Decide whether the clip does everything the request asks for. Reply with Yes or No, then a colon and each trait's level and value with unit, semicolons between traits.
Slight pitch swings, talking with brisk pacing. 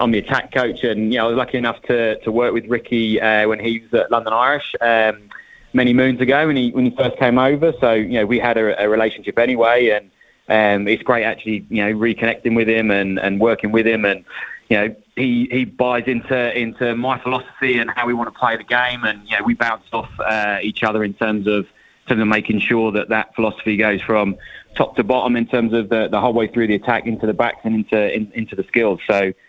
Yes: narrow, 2.0 semitones; fast, 250 wpm